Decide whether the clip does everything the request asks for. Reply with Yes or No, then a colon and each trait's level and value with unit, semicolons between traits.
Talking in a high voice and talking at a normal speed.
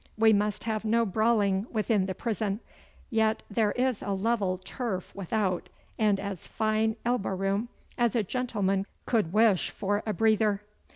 Yes: high, 215 Hz; average, 155 wpm